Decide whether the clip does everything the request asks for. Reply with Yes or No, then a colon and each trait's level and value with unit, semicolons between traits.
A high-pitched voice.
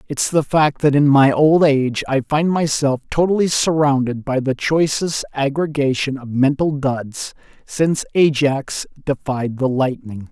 No: medium, 140 Hz